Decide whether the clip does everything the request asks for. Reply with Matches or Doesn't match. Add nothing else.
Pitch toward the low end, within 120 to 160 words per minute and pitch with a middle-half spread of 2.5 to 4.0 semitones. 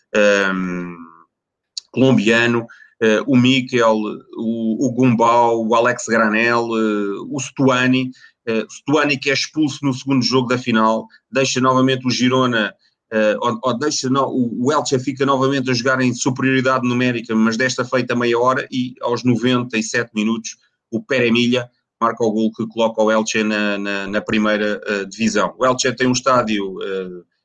Matches